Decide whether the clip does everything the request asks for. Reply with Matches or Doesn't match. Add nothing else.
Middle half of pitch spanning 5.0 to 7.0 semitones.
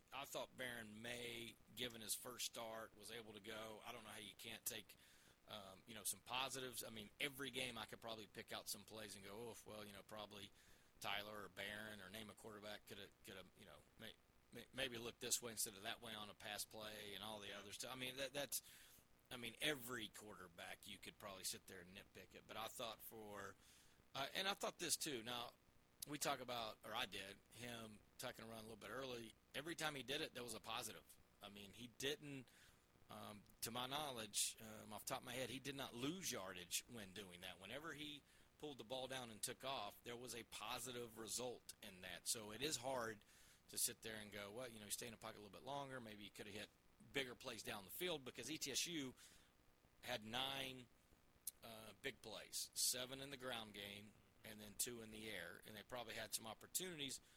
Doesn't match